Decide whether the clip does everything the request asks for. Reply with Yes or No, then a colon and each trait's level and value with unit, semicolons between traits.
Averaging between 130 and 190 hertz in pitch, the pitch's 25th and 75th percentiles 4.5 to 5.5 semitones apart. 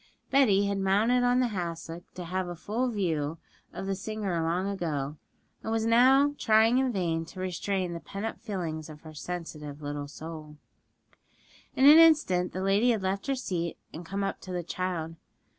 Yes: medium, 185 Hz; average, 4.9 semitones